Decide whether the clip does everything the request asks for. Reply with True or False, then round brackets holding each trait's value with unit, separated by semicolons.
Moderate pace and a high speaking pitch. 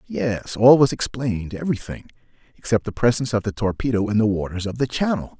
False (180 wpm; 115 Hz)